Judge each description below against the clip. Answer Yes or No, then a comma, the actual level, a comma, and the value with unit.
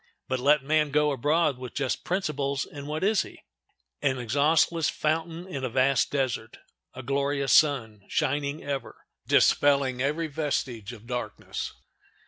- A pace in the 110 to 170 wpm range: Yes, average, 140 wpm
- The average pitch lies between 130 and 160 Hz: Yes, medium, 140 Hz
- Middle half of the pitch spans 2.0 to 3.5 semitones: Yes, average, 2.7 semitones